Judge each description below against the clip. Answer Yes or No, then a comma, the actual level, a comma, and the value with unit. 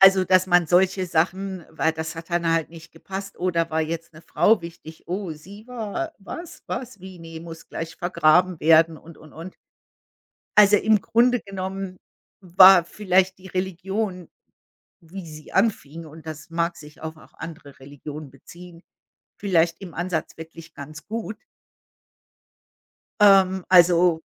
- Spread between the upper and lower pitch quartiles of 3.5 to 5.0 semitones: No, average, 2.9 semitones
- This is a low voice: No, medium, 175 Hz